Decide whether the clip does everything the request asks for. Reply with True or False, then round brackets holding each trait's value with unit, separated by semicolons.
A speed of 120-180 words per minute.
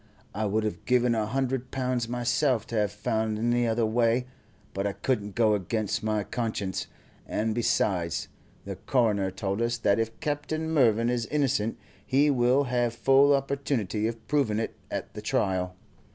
True (165 wpm)